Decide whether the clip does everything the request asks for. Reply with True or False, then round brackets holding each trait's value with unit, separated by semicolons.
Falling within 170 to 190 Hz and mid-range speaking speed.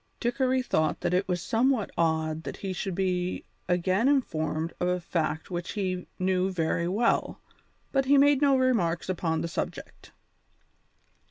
True (185 Hz; 155 wpm)